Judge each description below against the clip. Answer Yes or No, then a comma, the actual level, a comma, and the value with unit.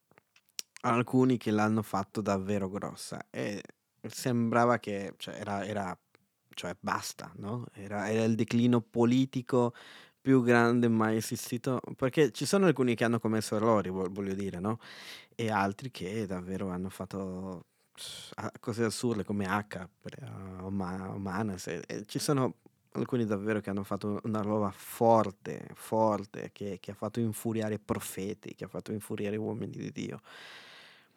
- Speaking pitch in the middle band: No, low, 110 Hz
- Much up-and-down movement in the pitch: No, average, 3.0 semitones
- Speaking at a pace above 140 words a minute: No, average, 135 wpm